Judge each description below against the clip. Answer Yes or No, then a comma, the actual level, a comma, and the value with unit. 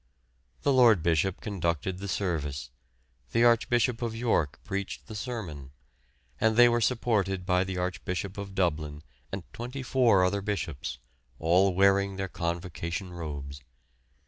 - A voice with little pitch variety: No, average, 4.6 semitones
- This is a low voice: Yes, very low, 95 Hz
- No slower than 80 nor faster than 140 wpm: Yes, slow, 135 wpm